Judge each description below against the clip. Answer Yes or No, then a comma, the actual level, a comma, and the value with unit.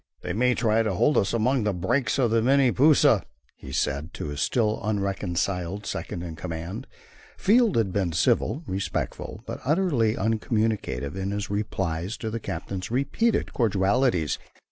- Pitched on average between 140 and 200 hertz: No, low, 105 Hz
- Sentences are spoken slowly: No, average, 155 wpm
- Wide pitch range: No, average, 5.0 semitones